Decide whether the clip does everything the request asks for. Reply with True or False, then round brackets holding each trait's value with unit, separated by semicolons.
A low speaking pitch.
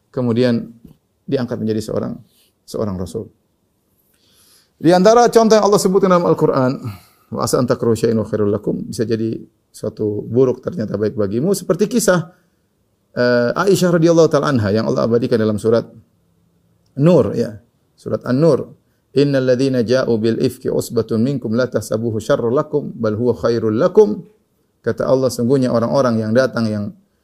True (120 Hz)